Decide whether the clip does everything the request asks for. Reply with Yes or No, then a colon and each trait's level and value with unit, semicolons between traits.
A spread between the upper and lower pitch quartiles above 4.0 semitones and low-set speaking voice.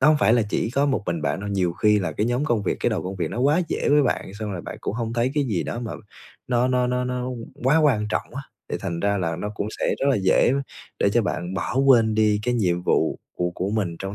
Yes: average, 4.7 semitones; low, 110 Hz